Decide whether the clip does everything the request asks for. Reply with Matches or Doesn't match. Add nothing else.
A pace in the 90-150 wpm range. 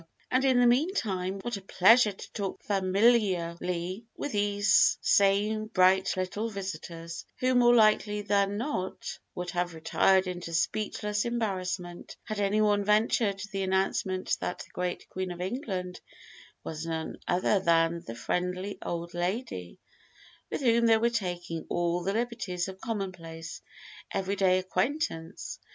Matches